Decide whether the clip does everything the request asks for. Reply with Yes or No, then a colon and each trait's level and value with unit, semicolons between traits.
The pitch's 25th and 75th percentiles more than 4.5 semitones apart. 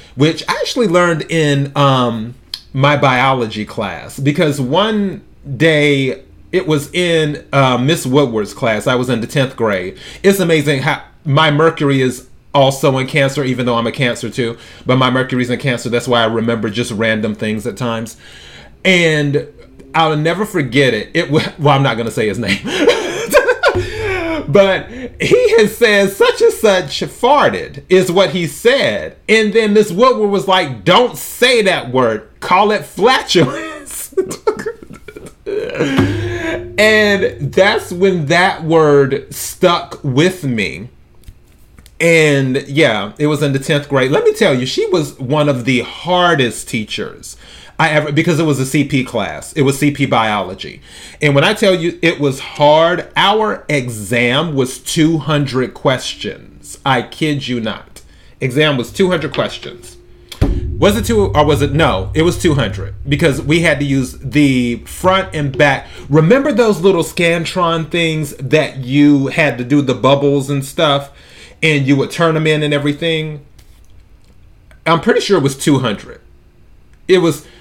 Yes: average, 5.0 semitones